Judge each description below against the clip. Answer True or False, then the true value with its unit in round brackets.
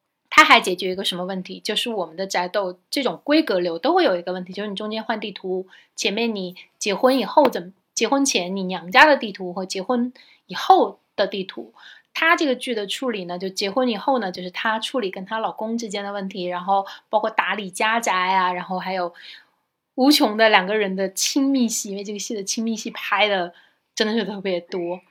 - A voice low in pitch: False (205 Hz)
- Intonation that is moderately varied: True (3.9 semitones)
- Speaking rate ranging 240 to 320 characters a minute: True (315 characters per minute)